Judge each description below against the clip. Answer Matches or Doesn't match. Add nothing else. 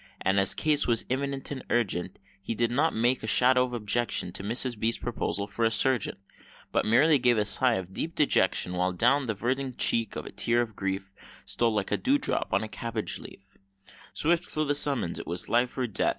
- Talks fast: Matches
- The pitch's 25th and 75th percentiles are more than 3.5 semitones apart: Matches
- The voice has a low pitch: Matches